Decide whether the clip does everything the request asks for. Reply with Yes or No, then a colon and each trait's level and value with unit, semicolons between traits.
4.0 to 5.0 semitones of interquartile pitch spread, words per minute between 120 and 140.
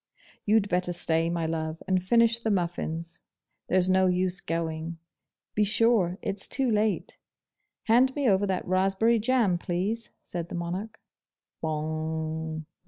Yes: average, 4.3 semitones; slow, 135 wpm